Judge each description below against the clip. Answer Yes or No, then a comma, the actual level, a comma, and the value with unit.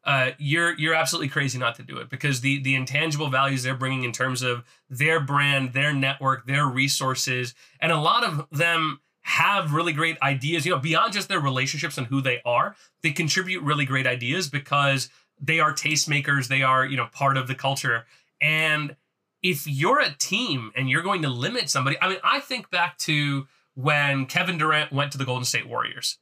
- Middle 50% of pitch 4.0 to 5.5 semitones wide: No, average, 3.2 semitones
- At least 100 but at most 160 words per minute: No, average, 200 wpm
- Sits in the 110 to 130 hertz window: No, medium, 140 Hz